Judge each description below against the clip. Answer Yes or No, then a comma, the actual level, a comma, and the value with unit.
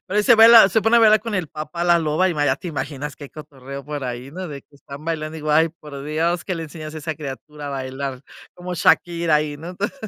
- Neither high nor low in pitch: Yes, medium, 155 Hz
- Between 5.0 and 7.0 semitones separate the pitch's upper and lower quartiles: No, average, 3.4 semitones